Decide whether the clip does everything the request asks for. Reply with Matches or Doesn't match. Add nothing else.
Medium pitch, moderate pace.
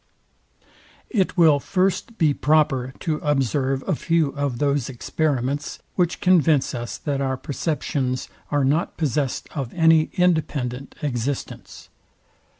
Doesn't match